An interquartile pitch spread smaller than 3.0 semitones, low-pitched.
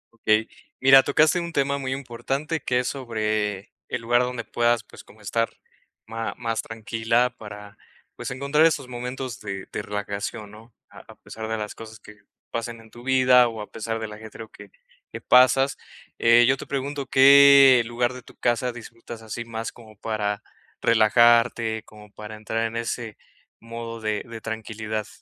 Yes: narrow, 2.5 semitones; low, 115 Hz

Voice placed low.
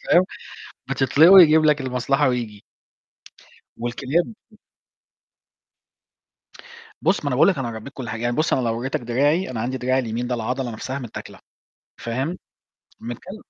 Yes: low, 130 Hz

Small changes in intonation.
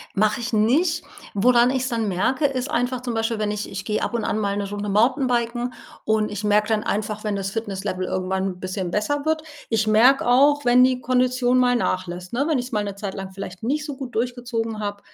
No: average, 3.6 semitones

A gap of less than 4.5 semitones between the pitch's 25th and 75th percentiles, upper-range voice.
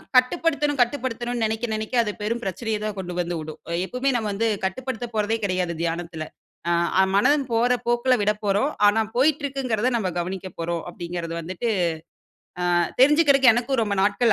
No: average, 5.0 semitones; high, 220 Hz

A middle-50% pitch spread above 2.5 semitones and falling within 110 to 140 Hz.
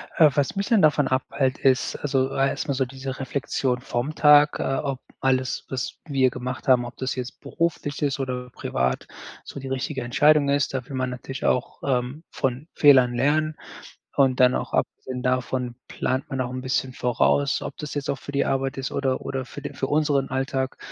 No: narrow, 1.8 semitones; low, 135 Hz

